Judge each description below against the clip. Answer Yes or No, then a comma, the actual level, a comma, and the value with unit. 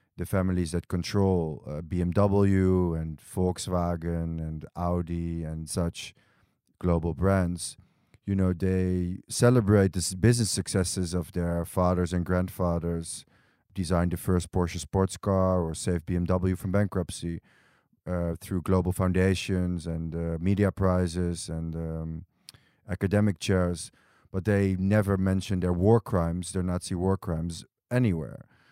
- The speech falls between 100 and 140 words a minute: Yes, average, 130 wpm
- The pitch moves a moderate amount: No, narrow, 1.9 semitones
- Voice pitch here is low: Yes, very low, 90 Hz